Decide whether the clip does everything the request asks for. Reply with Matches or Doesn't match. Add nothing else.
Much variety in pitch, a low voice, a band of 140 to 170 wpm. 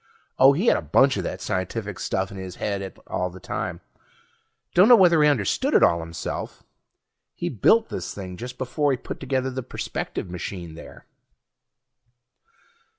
Matches